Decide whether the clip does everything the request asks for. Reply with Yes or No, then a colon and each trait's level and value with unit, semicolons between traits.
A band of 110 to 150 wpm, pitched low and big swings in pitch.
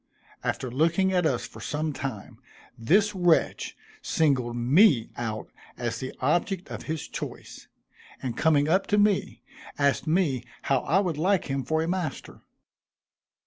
No: average, 145 wpm; medium, 155 Hz; wide, 5.8 semitones